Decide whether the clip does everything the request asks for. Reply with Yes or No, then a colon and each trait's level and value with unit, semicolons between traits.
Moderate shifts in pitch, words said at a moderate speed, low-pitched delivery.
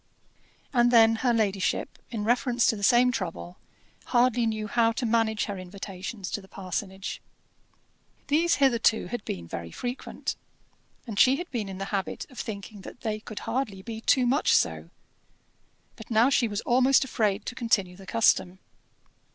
No: average, 3.8 semitones; average, 165 wpm; high, 220 Hz